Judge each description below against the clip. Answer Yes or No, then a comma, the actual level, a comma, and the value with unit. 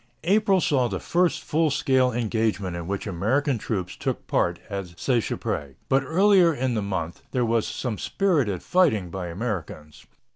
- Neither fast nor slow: Yes, average, 155 wpm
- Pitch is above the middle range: No, low, 115 Hz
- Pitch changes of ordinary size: No, wide, 7.4 semitones